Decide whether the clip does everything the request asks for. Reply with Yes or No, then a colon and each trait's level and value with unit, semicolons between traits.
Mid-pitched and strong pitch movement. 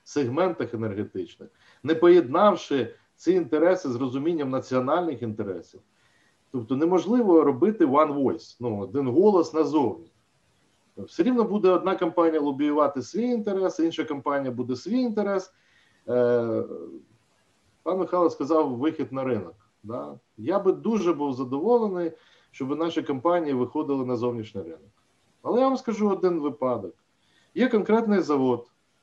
Yes: medium, 155 Hz; wide, 6.3 semitones